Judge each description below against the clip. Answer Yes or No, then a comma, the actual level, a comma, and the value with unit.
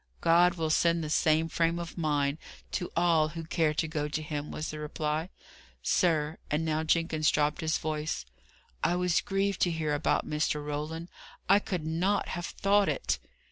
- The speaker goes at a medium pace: Yes, average, 180 wpm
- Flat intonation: Yes, narrow, 2.1 semitones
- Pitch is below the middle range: No, medium, 160 Hz